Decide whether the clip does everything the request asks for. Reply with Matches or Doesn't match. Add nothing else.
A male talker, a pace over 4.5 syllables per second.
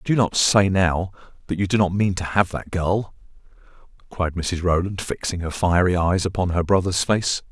Matches